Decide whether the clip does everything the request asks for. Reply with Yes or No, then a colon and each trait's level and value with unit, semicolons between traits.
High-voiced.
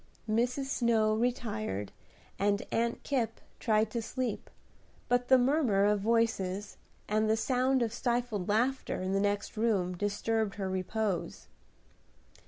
Yes: high, 220 Hz